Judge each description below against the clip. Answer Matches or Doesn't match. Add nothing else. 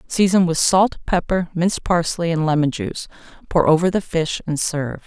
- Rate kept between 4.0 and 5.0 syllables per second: Doesn't match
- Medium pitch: Matches